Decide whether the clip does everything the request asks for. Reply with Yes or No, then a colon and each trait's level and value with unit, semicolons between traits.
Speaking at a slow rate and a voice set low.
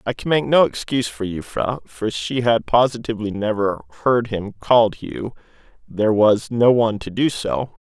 No: average, 175 wpm; low, 110 Hz